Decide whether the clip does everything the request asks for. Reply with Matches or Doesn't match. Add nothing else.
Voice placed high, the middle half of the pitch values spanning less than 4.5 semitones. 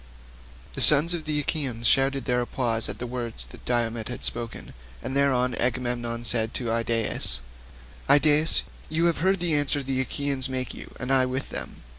Doesn't match